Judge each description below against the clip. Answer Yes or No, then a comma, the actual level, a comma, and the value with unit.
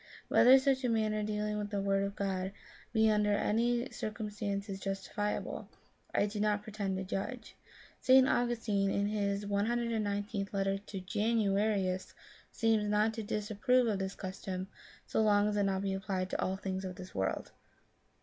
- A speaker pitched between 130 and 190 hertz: No, high, 205 Hz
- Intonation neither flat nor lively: No, narrow, 1.8 semitones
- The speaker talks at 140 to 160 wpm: No, average, 170 wpm